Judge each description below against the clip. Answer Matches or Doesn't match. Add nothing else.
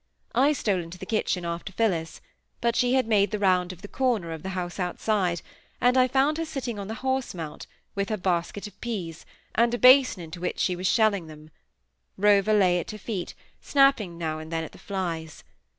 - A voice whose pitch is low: Doesn't match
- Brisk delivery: Matches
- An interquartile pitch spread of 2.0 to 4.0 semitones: Doesn't match